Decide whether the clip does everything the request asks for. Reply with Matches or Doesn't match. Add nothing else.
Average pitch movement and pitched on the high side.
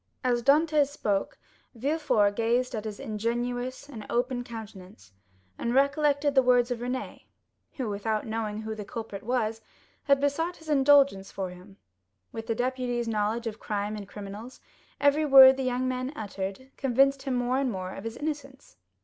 Matches